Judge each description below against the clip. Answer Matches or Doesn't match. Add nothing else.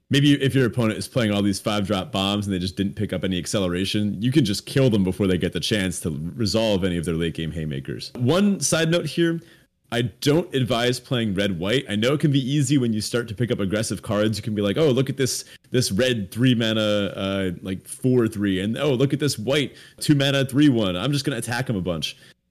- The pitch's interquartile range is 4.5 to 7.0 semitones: Matches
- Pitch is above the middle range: Doesn't match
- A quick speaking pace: Matches